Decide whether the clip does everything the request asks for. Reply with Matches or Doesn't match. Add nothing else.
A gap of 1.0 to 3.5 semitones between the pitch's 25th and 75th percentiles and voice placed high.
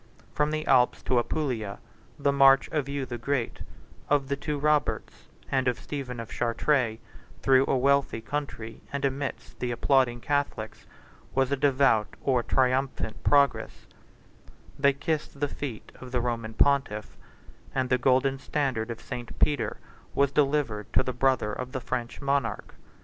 Doesn't match